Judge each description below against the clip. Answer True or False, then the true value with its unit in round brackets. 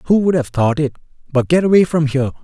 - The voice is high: False (150 Hz)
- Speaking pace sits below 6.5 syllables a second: False (6.6 syllables/s)